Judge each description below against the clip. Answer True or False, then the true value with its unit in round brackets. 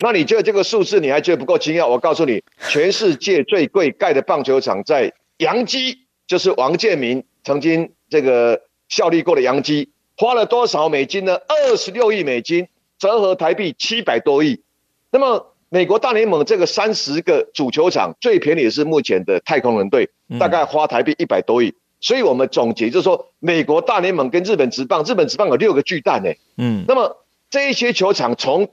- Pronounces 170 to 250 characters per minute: False (300 characters per minute)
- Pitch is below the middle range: False (240 Hz)